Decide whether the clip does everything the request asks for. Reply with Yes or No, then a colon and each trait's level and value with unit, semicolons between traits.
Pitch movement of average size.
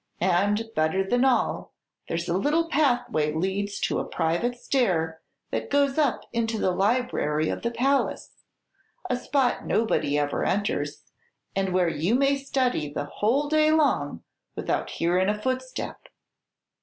No: wide, 7.2 semitones